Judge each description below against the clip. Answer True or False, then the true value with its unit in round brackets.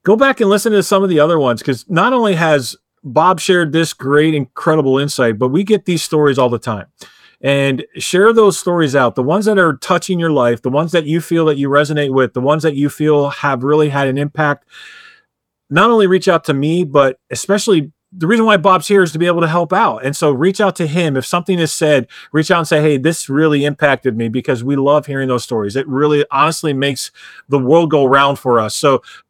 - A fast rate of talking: True (235 wpm)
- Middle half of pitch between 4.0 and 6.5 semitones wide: True (4.4 semitones)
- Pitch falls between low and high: True (150 Hz)